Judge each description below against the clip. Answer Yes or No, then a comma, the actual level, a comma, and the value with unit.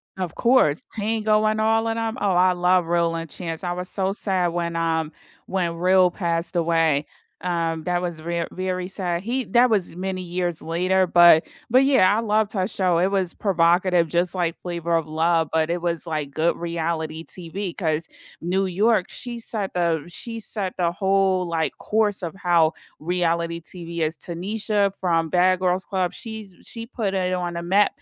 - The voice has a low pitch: No, medium, 180 Hz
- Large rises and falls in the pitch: No, narrow, 2.6 semitones